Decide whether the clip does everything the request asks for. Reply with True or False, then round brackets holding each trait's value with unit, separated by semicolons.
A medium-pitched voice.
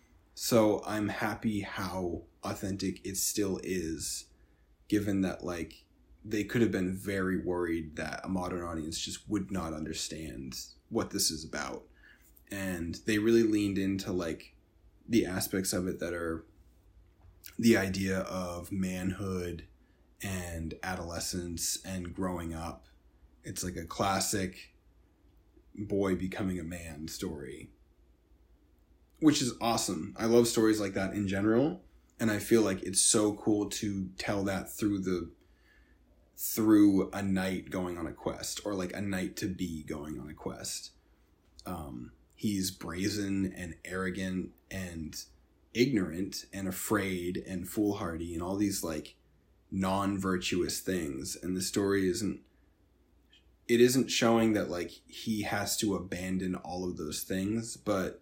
False (95 Hz)